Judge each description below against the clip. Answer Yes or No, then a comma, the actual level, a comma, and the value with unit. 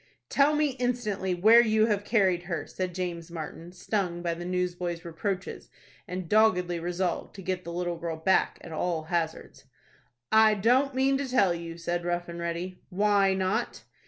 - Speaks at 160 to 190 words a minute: Yes, average, 170 wpm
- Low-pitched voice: No, medium, 180 Hz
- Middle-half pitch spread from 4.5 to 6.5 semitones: No, average, 3.6 semitones